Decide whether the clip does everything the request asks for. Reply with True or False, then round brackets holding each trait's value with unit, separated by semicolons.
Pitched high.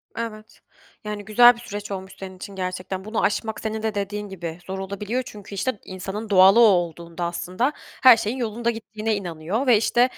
True (205 Hz)